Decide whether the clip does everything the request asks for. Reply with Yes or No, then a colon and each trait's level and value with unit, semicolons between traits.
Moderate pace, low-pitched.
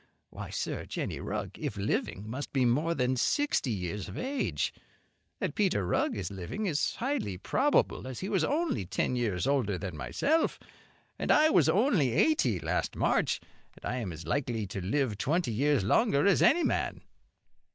Yes: average, 170 wpm; low, 130 Hz